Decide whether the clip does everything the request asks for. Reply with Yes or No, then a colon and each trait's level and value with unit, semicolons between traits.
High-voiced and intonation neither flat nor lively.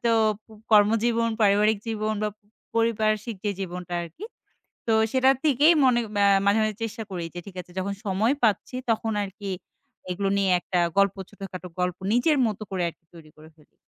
Yes: high, 205 Hz; average, 3.3 semitones